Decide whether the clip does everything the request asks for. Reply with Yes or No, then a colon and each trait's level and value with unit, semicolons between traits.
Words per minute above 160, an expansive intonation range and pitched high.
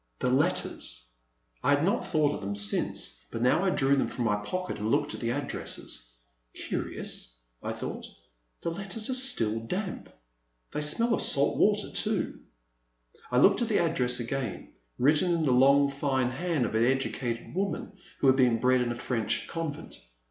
No: average, 175 wpm; wide, 6.3 semitones; low, 135 Hz